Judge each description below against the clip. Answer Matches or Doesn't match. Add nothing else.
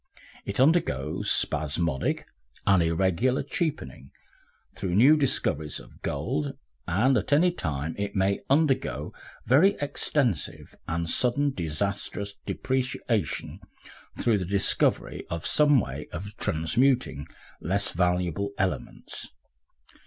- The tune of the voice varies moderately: Doesn't match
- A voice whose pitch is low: Matches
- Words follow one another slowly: Matches